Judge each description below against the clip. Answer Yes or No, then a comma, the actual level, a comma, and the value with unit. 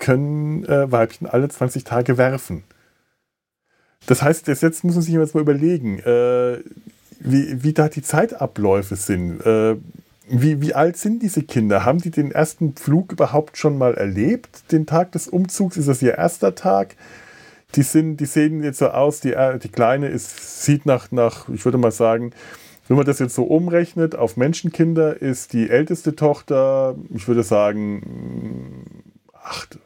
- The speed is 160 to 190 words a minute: Yes, average, 165 wpm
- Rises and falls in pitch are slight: No, average, 4.7 semitones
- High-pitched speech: No, low, 135 Hz